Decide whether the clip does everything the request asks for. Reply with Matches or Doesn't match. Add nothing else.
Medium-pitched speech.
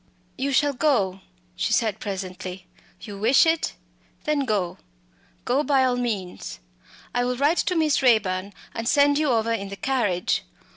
Doesn't match